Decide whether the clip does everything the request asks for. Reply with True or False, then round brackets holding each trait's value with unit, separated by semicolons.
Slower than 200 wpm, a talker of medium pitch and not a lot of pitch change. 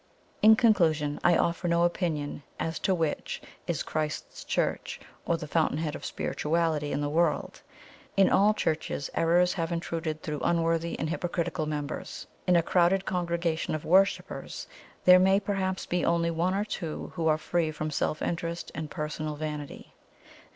True (160 wpm; 165 Hz; 2.3 semitones)